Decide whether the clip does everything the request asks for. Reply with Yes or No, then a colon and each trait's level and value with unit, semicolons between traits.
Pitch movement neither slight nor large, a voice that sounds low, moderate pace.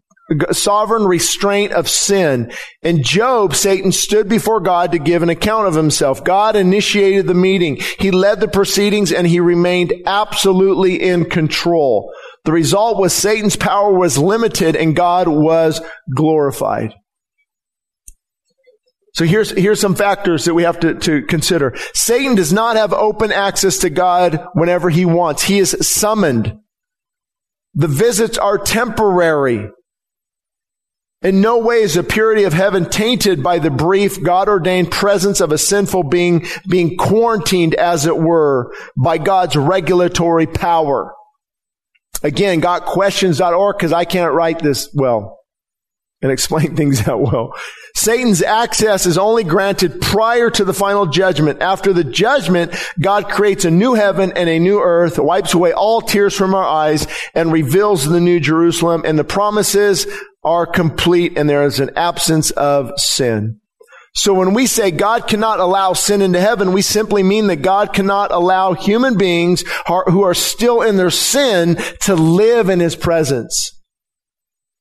No: average, 3.3 semitones; medium, 185 Hz; average, 150 wpm